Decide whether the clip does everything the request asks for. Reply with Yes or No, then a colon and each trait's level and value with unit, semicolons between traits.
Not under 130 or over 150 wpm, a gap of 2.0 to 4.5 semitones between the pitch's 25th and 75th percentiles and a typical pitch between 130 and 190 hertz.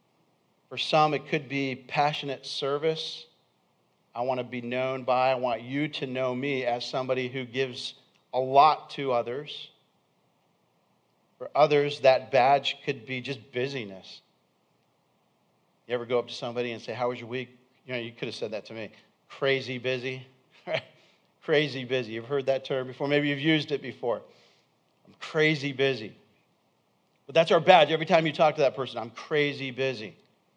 No: average, 170 wpm; narrow, 2.4 semitones; low, 135 Hz